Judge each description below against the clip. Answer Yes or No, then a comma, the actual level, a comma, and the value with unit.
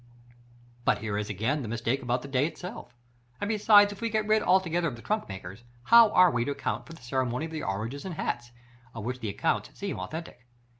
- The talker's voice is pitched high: No, low, 135 Hz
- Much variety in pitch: Yes, wide, 7.6 semitones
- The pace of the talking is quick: Yes, fast, 215 wpm